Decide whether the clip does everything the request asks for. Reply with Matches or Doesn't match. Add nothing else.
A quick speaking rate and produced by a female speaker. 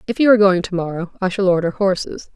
Matches